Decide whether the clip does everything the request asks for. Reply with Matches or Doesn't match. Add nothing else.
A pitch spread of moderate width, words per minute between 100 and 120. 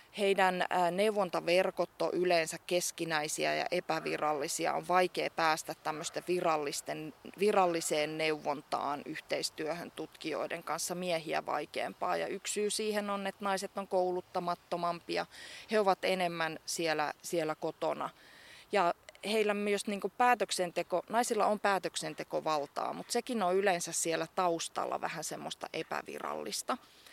Matches